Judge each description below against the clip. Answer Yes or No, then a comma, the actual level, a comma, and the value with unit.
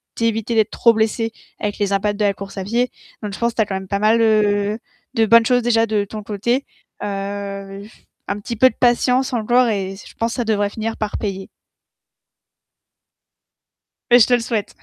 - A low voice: No, high, 215 Hz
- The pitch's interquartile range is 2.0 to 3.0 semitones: Yes, narrow, 2.4 semitones